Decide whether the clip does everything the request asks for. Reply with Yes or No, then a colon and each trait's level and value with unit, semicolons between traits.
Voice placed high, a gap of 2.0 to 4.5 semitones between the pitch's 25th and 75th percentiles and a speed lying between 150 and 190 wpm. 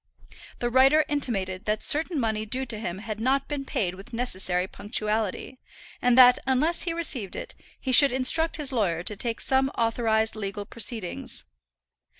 Yes: high, 235 Hz; average, 4.1 semitones; average, 160 wpm